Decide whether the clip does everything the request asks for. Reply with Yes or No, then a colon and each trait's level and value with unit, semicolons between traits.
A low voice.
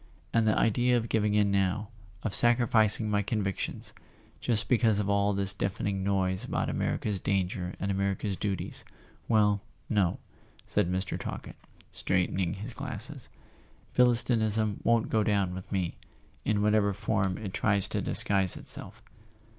Yes: low, 100 Hz